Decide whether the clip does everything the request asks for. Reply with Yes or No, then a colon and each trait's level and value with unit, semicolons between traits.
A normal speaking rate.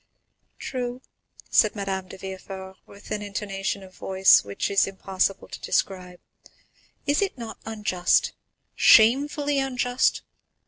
No: slow, 120 wpm